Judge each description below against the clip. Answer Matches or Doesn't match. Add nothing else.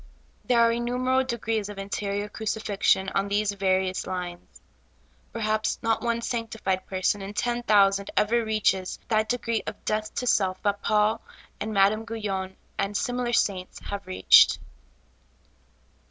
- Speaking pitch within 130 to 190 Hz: Doesn't match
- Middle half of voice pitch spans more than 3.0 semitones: Doesn't match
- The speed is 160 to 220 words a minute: Doesn't match